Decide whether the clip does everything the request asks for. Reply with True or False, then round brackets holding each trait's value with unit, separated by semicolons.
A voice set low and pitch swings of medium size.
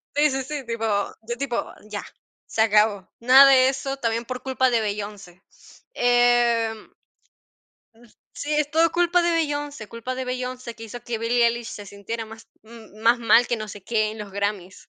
False (235 Hz; 3.3 semitones)